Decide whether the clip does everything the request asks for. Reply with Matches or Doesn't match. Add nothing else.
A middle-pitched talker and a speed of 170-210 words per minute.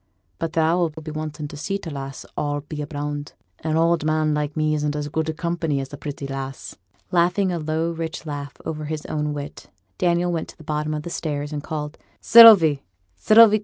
Matches